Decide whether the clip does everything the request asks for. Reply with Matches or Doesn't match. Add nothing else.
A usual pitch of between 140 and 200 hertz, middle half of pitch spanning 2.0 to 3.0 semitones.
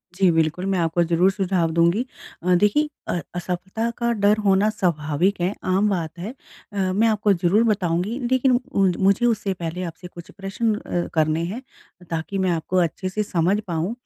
Doesn't match